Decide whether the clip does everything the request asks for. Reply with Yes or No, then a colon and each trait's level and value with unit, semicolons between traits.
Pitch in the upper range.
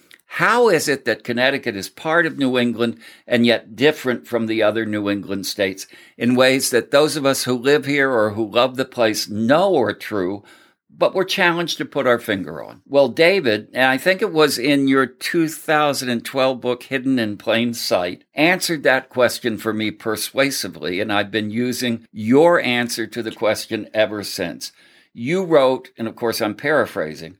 No: low, 125 Hz